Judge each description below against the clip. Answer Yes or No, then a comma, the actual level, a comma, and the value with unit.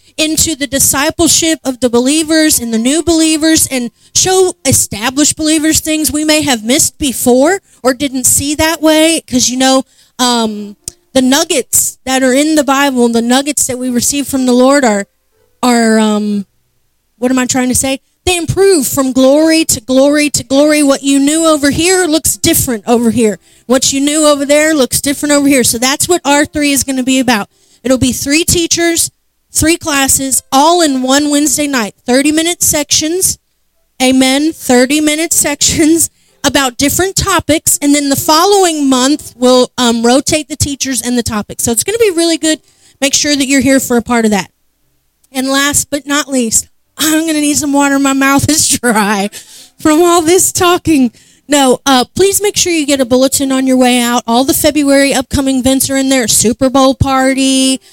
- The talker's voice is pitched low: No, very high, 275 Hz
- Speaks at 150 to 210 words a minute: Yes, average, 190 wpm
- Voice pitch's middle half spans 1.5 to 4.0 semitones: Yes, average, 3.5 semitones